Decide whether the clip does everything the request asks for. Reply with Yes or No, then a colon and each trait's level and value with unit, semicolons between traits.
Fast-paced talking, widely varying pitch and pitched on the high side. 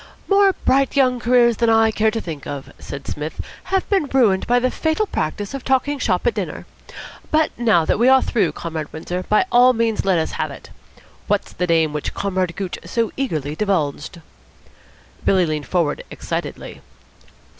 No: average, 175 wpm; wide, 7.2 semitones; high, 215 Hz